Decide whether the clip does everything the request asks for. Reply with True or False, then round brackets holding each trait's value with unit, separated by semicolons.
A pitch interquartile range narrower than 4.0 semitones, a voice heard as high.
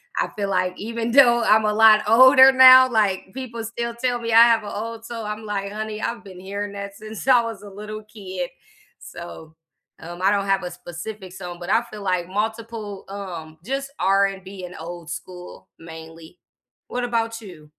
True (3.6 semitones; 210 Hz)